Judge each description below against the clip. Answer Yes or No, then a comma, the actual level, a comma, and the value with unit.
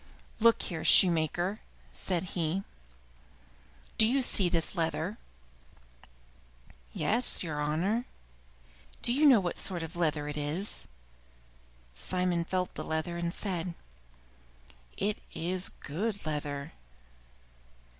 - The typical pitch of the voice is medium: Yes, medium, 175 Hz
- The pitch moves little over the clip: No, average, 3.9 semitones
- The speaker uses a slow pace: Yes, slow, 110 wpm